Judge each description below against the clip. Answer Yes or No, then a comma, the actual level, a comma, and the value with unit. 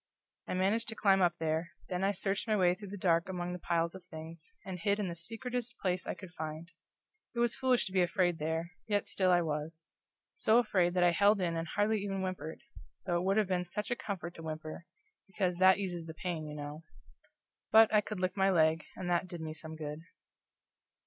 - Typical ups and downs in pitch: Yes, average, 3.1 semitones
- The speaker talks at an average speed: No, fast, 220 wpm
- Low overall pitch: No, medium, 180 Hz